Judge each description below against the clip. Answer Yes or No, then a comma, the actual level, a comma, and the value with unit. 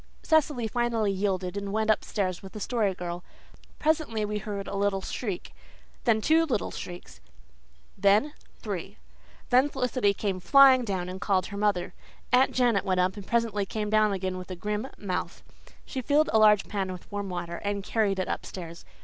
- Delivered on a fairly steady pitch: No, average, 3.5 semitones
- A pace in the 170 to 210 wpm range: Yes, average, 175 wpm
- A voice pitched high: Yes, high, 205 Hz